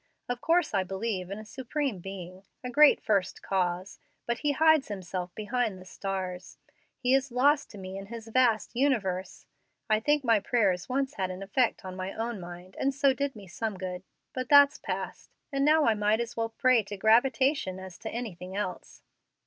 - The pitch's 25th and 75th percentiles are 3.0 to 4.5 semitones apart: No, wide, 5.5 semitones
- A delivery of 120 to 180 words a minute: No, average, 190 wpm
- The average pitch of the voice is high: Yes, high, 220 Hz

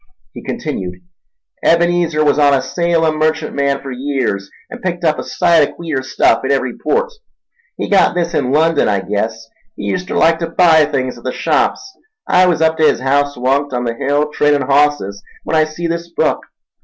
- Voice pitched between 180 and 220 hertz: No, medium, 150 Hz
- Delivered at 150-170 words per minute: No, average, 190 wpm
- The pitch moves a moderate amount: Yes, average, 4.1 semitones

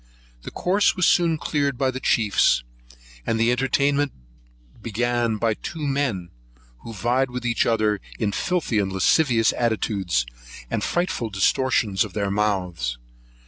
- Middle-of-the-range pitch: No, low, 115 Hz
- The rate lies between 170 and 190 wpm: No, slow, 135 wpm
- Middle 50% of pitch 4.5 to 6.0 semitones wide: Yes, average, 4.8 semitones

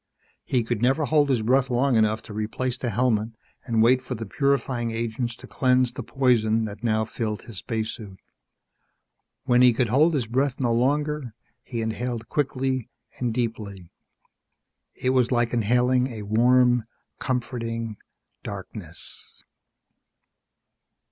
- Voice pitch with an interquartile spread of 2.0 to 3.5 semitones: Yes, narrow, 2.4 semitones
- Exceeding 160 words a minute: No, slow, 135 wpm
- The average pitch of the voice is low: Yes, low, 120 Hz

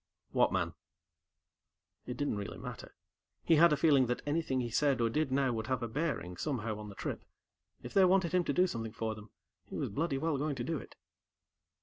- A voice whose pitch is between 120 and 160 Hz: Yes, low, 135 Hz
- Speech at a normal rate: No, fast, 215 wpm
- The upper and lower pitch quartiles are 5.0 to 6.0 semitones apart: Yes, wide, 5.5 semitones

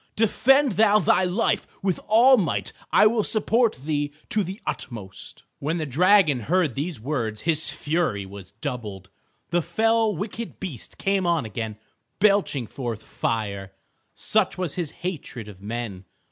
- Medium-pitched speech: Yes, medium, 160 Hz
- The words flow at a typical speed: Yes, average, 145 wpm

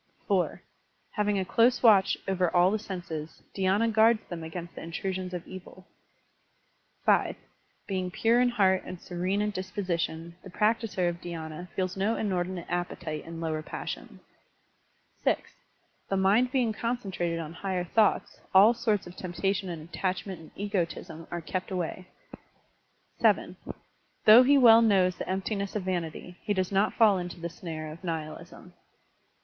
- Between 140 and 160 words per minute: Yes, average, 150 wpm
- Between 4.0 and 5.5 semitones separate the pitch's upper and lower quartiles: No, average, 3.1 semitones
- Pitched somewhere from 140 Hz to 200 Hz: Yes, medium, 185 Hz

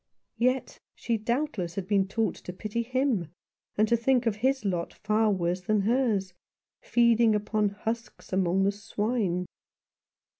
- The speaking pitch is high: Yes, high, 215 Hz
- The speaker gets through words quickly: No, average, 140 wpm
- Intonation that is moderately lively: Yes, average, 3.4 semitones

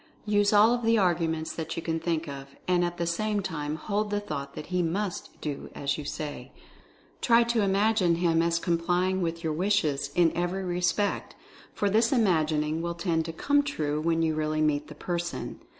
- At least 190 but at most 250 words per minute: Yes, average, 195 wpm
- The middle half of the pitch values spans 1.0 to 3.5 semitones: No, average, 4.2 semitones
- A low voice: No, medium, 170 Hz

